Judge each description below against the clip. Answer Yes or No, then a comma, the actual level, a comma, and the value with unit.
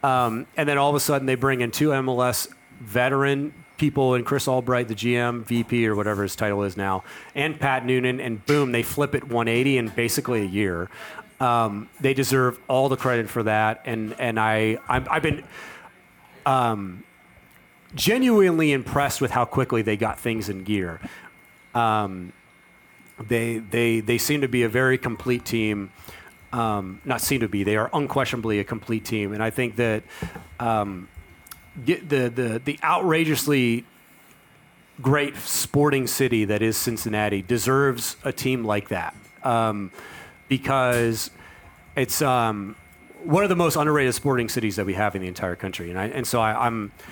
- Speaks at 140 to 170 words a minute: Yes, average, 165 wpm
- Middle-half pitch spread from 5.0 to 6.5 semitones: No, average, 3.8 semitones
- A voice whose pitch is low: Yes, low, 120 Hz